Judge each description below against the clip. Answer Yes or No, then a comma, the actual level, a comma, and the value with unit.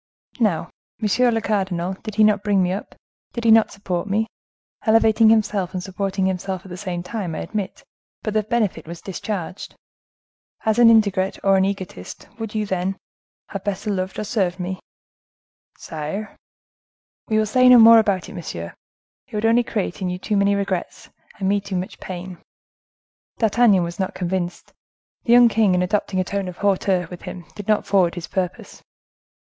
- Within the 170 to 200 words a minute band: Yes, average, 180 wpm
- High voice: Yes, high, 195 Hz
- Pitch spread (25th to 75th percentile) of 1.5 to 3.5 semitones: Yes, average, 2.8 semitones